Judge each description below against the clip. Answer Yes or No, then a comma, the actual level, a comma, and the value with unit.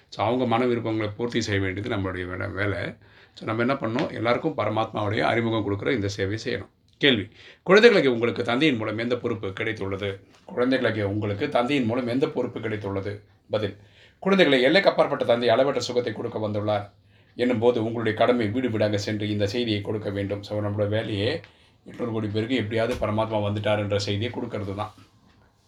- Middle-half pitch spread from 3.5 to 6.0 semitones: No, average, 2.7 semitones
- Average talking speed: No, fast, 160 wpm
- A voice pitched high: No, low, 110 Hz